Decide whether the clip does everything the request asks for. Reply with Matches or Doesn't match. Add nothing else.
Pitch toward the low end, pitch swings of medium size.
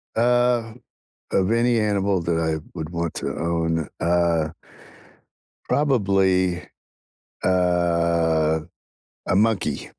Matches